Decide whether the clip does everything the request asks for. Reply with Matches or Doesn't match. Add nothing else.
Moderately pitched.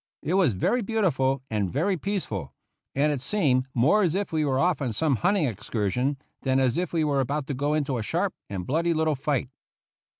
Matches